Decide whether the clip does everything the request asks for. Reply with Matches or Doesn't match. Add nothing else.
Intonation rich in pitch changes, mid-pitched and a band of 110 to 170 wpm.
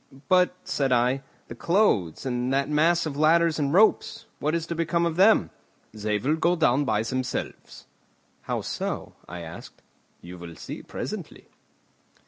Matches